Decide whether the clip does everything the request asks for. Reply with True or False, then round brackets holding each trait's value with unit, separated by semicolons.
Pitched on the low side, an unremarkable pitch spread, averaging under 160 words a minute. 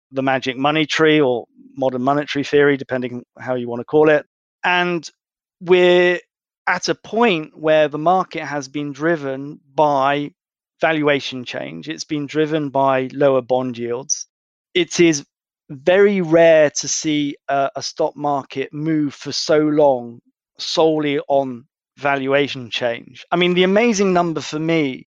False (150 Hz; 3.0 semitones; 145 wpm)